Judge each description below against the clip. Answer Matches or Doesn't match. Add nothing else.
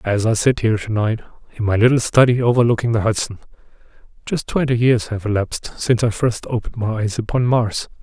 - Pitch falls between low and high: Doesn't match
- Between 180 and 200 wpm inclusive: Matches